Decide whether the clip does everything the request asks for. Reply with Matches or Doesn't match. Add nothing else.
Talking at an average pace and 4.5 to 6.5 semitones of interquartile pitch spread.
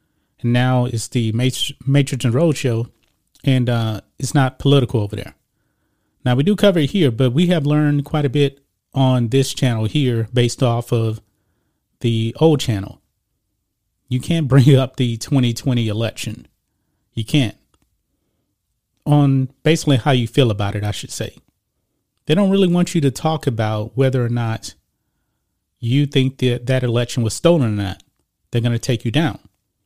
Doesn't match